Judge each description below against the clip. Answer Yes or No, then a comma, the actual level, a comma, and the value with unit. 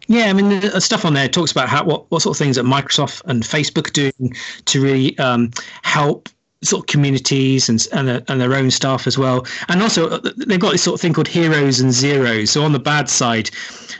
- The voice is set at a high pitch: No, medium, 140 Hz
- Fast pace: Yes, fast, 225 wpm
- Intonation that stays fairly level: No, average, 4.6 semitones